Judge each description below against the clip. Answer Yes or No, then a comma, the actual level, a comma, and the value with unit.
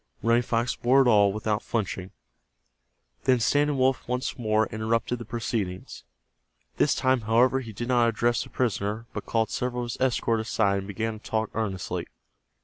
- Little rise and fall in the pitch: Yes, narrow, 2.3 semitones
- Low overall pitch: Yes, low, 115 Hz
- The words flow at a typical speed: Yes, average, 170 wpm